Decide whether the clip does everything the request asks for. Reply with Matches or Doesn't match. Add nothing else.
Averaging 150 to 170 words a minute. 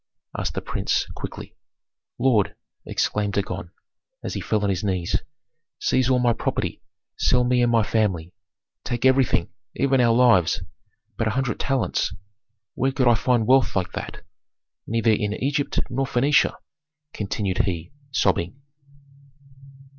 Doesn't match